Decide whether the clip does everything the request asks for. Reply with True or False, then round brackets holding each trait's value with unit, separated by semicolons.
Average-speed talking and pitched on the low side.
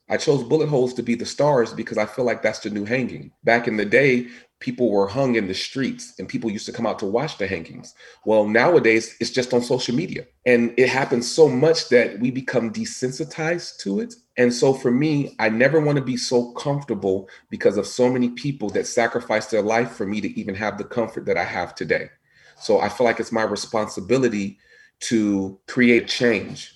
False (215 wpm; 120 Hz)